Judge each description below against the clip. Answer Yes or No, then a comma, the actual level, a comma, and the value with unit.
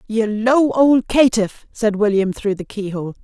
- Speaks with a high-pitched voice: Yes, high, 220 Hz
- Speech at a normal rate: Yes, average, 165 wpm